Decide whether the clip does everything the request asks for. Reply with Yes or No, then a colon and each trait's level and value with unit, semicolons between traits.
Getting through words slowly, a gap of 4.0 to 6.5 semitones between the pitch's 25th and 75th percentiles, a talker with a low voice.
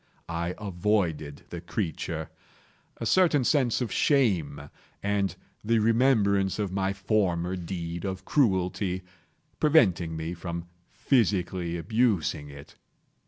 Yes: slow, 110 wpm; average, 4.3 semitones; very low, 95 Hz